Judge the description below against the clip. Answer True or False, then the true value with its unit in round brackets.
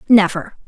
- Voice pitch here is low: False (200 Hz)